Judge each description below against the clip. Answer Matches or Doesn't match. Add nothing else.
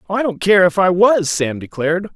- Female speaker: Doesn't match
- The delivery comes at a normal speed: Doesn't match